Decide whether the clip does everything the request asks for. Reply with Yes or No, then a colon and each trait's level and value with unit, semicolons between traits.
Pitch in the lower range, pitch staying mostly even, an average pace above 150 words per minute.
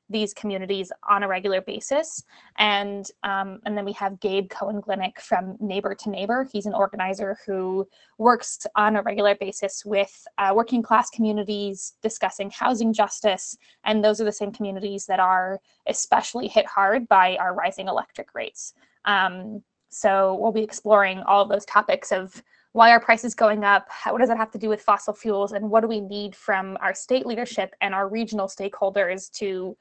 No: high, 205 Hz; narrow, 2.0 semitones; average, 180 wpm